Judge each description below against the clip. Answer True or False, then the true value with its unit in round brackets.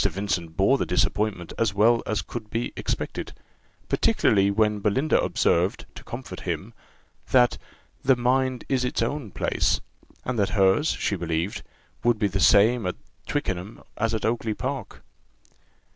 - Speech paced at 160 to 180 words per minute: False (145 wpm)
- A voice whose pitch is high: False (110 Hz)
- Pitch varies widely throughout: False (3.7 semitones)